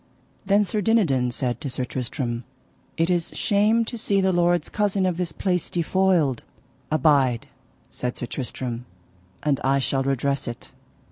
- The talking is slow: No, average, 150 wpm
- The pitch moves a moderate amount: No, wide, 6.6 semitones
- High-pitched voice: No, medium, 155 Hz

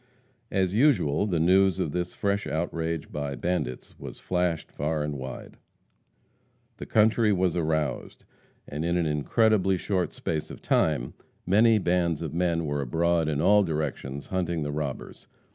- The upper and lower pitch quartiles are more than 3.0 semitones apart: Yes, average, 3.7 semitones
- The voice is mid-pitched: No, very low, 85 Hz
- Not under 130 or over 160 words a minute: Yes, average, 150 wpm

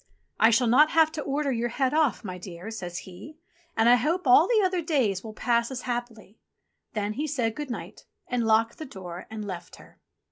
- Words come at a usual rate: No, fast, 210 wpm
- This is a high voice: Yes, high, 240 Hz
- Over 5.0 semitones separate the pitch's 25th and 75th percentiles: Yes, wide, 5.5 semitones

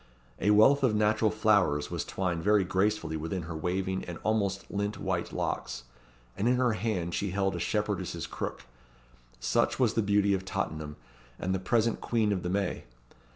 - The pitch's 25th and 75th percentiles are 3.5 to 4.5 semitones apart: No, average, 2.9 semitones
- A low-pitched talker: Yes, low, 100 Hz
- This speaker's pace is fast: No, average, 175 wpm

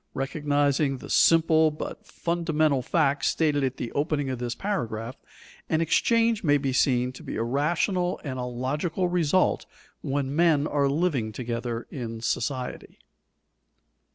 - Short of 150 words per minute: Yes, average, 140 wpm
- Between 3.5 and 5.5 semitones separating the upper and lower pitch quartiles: Yes, average, 4.2 semitones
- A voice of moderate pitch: Yes, medium, 145 Hz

